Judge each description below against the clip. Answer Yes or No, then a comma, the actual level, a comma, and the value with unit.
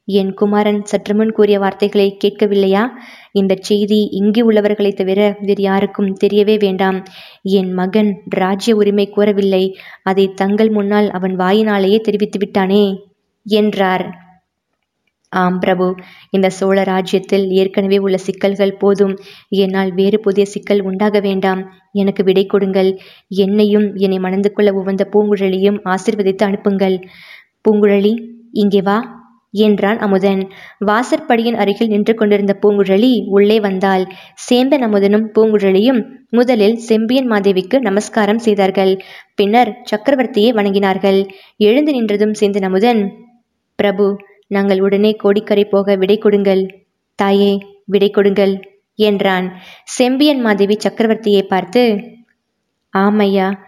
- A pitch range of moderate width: No, narrow, 1.5 semitones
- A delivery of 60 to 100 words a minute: No, average, 110 wpm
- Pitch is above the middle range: Yes, high, 200 Hz